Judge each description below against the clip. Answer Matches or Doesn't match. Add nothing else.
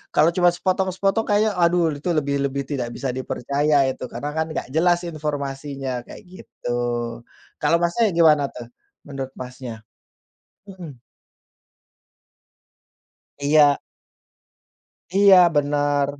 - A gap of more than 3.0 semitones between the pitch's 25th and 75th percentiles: Matches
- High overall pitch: Doesn't match